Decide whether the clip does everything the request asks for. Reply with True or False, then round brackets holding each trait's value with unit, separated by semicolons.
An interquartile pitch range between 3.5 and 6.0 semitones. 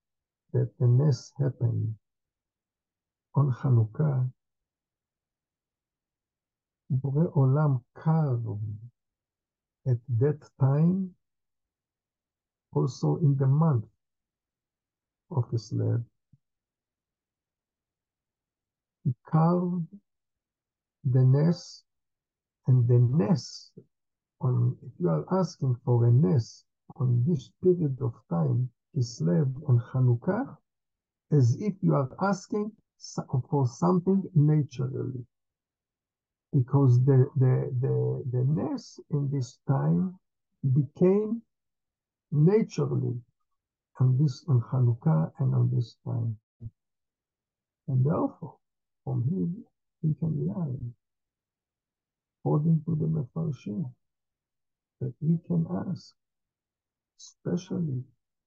True (5.2 semitones)